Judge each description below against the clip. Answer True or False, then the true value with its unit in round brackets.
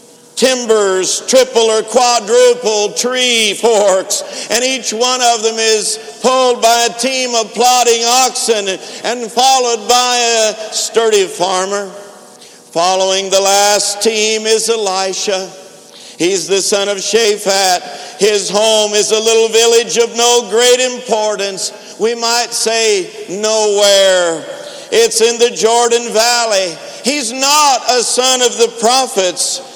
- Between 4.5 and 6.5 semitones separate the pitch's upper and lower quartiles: False (3.1 semitones)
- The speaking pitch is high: True (225 Hz)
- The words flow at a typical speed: False (125 wpm)